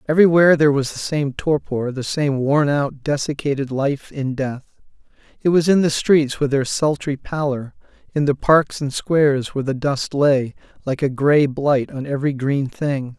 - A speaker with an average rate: Yes, average, 175 wpm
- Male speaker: Yes, male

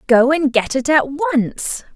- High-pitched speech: Yes, very high, 260 Hz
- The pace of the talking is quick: No, average, 185 wpm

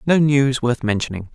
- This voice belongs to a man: Yes, male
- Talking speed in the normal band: Yes, average, 180 wpm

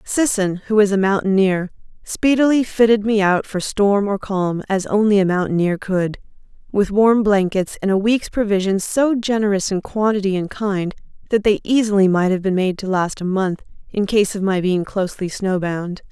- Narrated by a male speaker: No, female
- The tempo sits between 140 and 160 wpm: No, average, 180 wpm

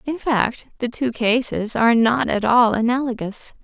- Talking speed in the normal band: Yes, average, 165 wpm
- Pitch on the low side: No, high, 235 Hz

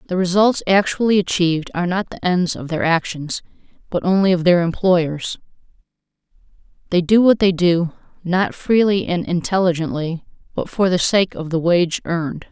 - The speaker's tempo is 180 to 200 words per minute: No, average, 160 wpm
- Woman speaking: Yes, female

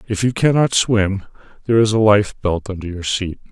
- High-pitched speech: No, low, 105 Hz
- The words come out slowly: No, fast, 205 wpm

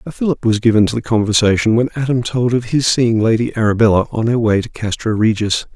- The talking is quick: Yes, fast, 220 wpm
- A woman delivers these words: No, male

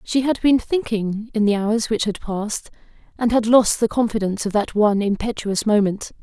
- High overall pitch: Yes, high, 215 Hz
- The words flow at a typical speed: Yes, average, 195 wpm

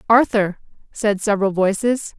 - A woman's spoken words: Yes, female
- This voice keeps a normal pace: No, slow, 110 wpm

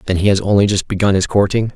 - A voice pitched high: No, low, 100 Hz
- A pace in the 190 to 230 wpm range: No, fast, 275 wpm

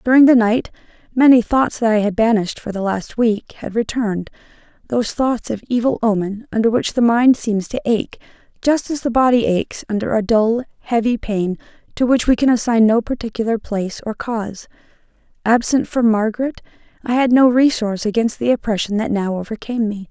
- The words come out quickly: No, average, 180 wpm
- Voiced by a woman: Yes, female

